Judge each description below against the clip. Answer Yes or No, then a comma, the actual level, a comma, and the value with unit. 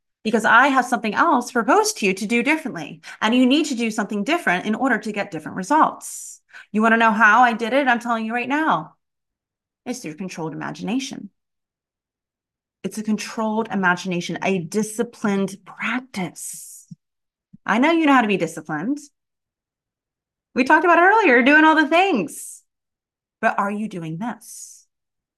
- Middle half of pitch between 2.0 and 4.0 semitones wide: No, average, 5.3 semitones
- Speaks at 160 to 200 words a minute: Yes, average, 165 wpm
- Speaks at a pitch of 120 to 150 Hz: No, high, 225 Hz